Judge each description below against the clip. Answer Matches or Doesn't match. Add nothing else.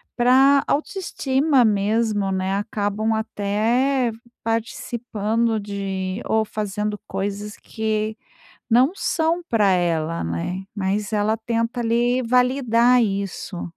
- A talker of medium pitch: Doesn't match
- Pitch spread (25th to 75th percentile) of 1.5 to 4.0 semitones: Matches